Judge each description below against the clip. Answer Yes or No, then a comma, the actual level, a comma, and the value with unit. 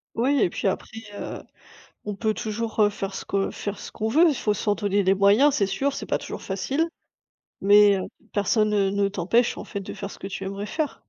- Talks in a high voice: Yes, high, 205 Hz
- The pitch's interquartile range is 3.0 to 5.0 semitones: No, narrow, 2.4 semitones